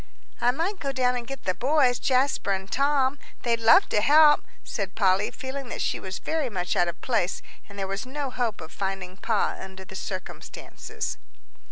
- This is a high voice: Yes, high, 235 Hz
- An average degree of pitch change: No, wide, 6.0 semitones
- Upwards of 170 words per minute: Yes, average, 190 wpm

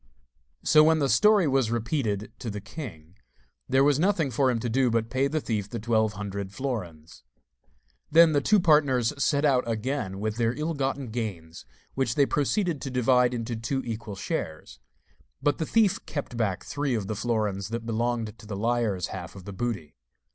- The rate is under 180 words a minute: No, average, 190 wpm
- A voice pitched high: No, low, 120 Hz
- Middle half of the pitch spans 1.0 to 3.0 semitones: No, average, 4.8 semitones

